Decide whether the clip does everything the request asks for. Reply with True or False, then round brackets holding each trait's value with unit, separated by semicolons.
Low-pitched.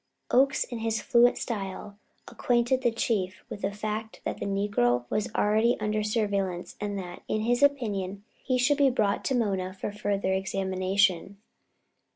False (210 Hz)